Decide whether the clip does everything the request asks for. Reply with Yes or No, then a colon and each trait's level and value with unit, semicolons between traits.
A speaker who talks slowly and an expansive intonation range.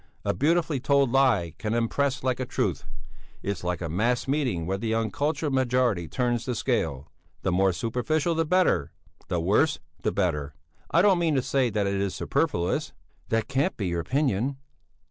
No: average, 175 wpm; wide, 6.6 semitones